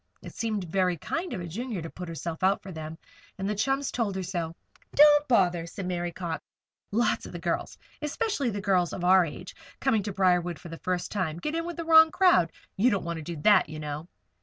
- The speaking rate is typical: No, fast, 225 wpm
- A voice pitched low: No, high, 190 Hz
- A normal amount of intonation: No, wide, 5.8 semitones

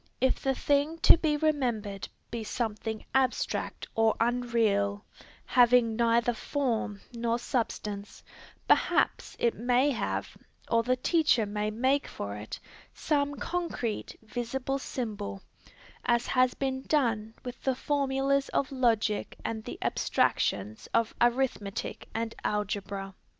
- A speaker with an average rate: No, slow, 120 wpm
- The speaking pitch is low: No, high, 235 Hz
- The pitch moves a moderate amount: Yes, average, 3.7 semitones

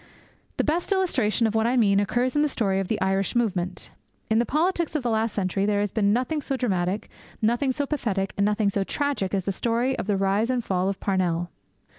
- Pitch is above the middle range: Yes, high, 215 Hz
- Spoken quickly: Yes, fast, 225 wpm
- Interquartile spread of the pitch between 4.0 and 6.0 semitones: Yes, average, 4.6 semitones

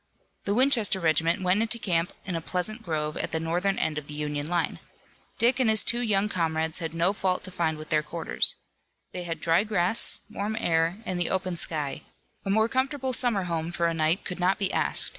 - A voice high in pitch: No, medium, 180 Hz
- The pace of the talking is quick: Yes, fast, 215 wpm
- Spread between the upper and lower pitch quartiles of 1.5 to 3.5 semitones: No, average, 4.3 semitones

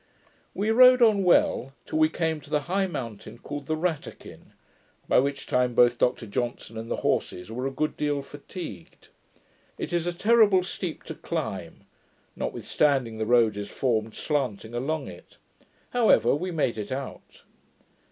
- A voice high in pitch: No, medium, 140 Hz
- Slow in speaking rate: No, average, 155 wpm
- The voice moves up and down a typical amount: No, wide, 6.4 semitones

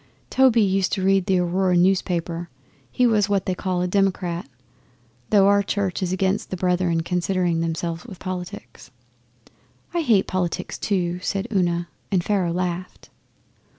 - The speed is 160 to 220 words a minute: No, average, 150 wpm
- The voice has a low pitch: No, medium, 185 Hz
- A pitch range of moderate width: No, narrow, 1.9 semitones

